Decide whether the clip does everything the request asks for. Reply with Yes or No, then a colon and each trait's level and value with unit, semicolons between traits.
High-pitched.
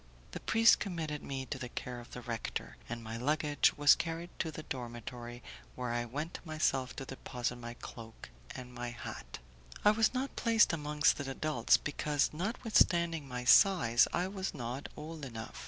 No: medium, 140 Hz